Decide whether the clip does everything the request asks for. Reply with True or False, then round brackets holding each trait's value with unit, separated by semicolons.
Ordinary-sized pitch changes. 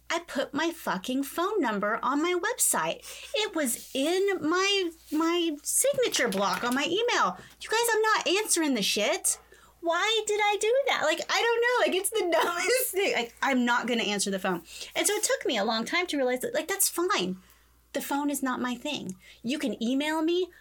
False (7.9 semitones)